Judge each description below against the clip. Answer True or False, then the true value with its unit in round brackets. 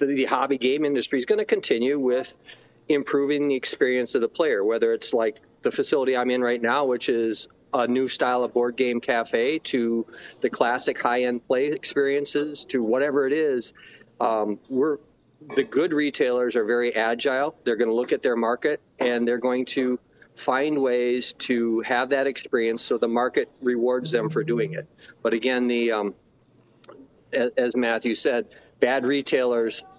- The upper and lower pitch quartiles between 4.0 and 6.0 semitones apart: False (2.8 semitones)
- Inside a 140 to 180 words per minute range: True (170 wpm)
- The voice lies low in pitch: True (125 Hz)